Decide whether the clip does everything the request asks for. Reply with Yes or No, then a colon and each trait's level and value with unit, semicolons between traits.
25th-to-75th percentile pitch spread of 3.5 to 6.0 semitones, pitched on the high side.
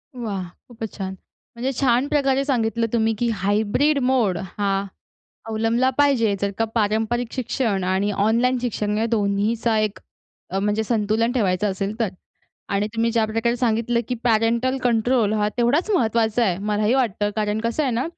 No: narrow, 2.6 semitones; high, 225 Hz